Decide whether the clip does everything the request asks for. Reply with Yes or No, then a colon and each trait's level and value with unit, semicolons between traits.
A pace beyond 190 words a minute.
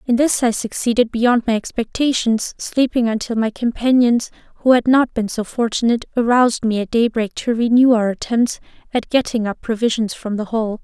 No: average, 175 wpm